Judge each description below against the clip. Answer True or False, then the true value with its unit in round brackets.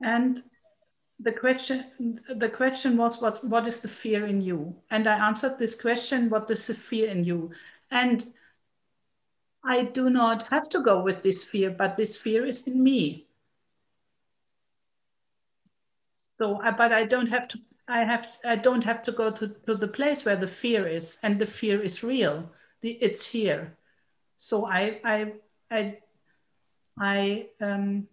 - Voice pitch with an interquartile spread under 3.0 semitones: True (2.6 semitones)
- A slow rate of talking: False (165 wpm)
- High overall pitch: True (225 Hz)